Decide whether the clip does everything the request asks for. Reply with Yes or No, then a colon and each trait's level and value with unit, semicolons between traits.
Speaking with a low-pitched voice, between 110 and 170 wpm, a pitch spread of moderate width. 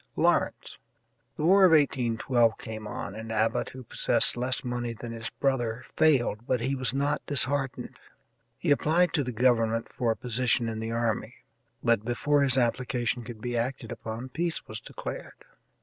Yes: low, 120 Hz; average, 165 wpm; average, 3.0 semitones